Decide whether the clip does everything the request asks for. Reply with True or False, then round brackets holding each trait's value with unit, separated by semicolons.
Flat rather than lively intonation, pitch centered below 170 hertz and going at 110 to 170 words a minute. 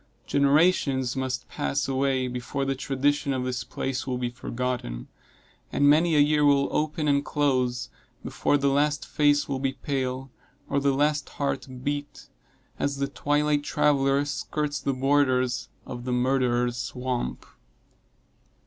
True (2.2 semitones; 135 Hz; 140 wpm)